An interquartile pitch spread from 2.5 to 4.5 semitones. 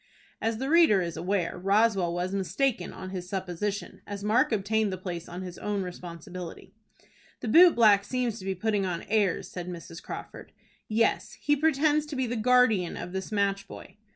Yes: average, 3.8 semitones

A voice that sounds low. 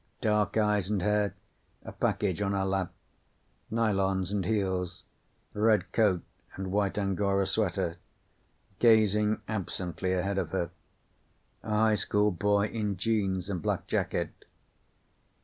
Yes: low, 100 Hz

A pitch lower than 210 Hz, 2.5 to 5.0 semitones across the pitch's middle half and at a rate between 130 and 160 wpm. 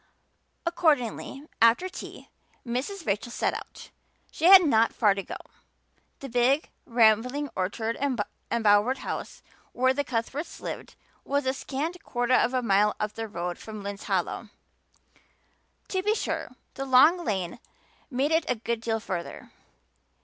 No: high, 245 Hz; average, 4.6 semitones; average, 140 wpm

